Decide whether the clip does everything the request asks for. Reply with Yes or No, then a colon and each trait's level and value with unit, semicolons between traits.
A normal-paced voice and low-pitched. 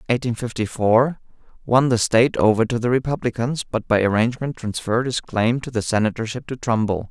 Yes: average, 170 wpm; low, 120 Hz